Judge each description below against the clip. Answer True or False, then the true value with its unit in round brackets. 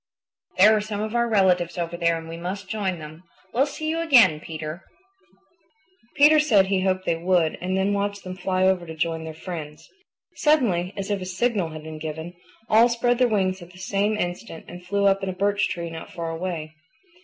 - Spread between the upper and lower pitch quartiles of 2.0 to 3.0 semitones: False (3.5 semitones)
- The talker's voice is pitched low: False (185 Hz)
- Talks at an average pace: False (210 wpm)